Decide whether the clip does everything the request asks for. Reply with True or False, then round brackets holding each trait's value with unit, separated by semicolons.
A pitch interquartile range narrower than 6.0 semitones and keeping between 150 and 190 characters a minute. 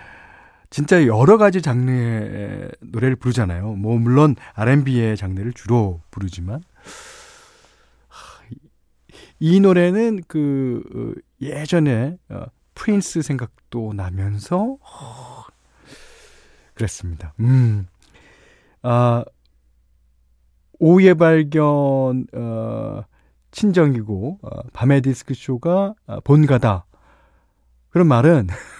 False (7.8 semitones; 165 characters per minute)